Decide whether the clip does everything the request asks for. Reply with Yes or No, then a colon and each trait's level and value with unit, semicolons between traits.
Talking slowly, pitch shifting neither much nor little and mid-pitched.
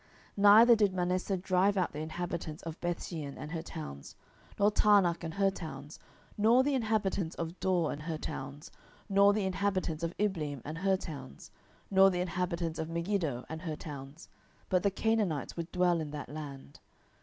No: average, 175 wpm; average, 3.9 semitones; medium, 175 Hz